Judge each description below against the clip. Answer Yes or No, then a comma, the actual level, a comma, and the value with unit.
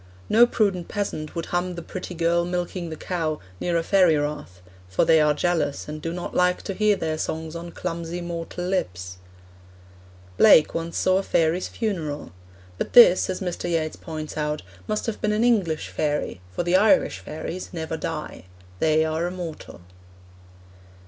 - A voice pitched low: No, medium, 170 Hz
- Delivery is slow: No, average, 170 wpm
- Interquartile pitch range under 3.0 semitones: Yes, narrow, 2.6 semitones